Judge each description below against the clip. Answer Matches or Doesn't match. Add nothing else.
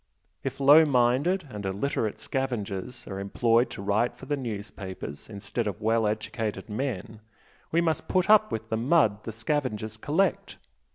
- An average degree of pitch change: Matches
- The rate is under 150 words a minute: Doesn't match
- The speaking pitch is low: Matches